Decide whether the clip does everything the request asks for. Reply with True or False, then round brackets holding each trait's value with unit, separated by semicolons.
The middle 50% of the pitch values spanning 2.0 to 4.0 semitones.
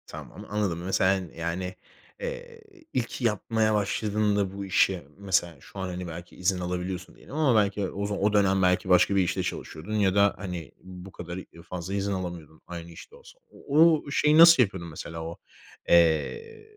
True (3.1 semitones)